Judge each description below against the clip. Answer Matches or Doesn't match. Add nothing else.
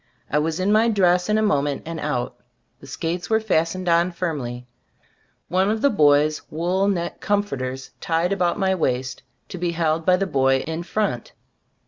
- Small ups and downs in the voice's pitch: Doesn't match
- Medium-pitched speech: Matches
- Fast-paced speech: Doesn't match